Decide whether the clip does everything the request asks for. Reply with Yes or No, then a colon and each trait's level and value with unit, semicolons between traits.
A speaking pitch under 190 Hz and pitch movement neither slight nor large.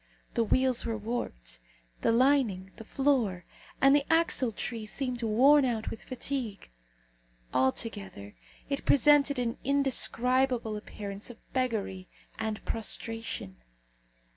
No: high, 230 Hz; average, 3.9 semitones